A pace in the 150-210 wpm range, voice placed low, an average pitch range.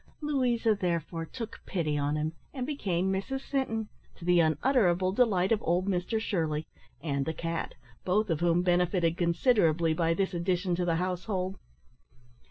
No: average, 155 wpm; medium, 180 Hz; average, 4.1 semitones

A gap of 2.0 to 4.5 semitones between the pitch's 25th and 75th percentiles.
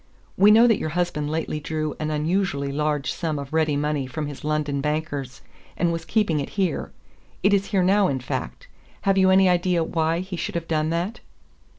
Yes: average, 3.6 semitones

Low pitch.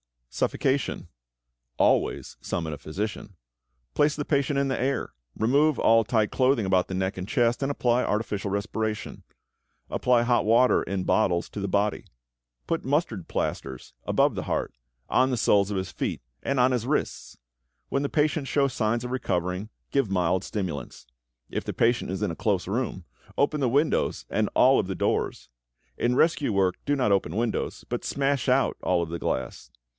Yes: low, 115 Hz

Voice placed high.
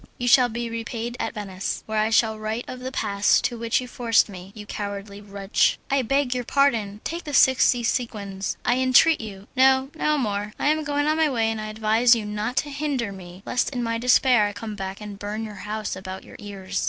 Yes: high, 225 Hz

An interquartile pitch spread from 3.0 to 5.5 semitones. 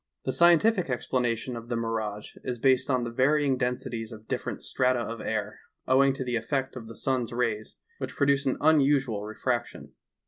No: narrow, 2.6 semitones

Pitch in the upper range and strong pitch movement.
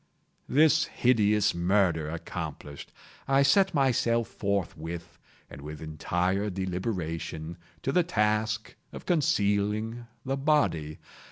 No: low, 105 Hz; wide, 6.6 semitones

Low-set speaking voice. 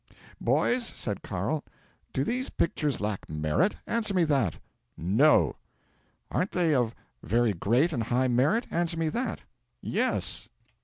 No: medium, 145 Hz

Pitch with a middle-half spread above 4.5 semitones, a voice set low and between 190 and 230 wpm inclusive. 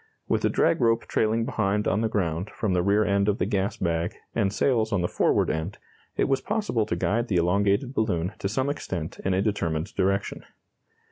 No: average, 3.4 semitones; low, 100 Hz; fast, 205 wpm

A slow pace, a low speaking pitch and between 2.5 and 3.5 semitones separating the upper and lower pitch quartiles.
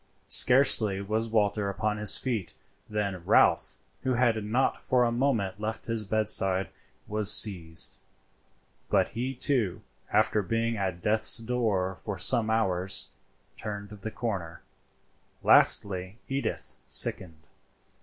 Yes: slow, 120 wpm; low, 105 Hz; average, 2.9 semitones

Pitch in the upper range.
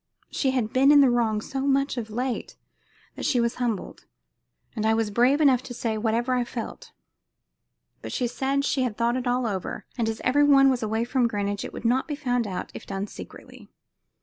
Yes: high, 245 Hz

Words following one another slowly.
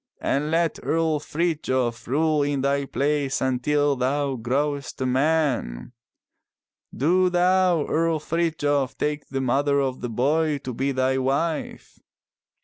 Yes: slow, 130 wpm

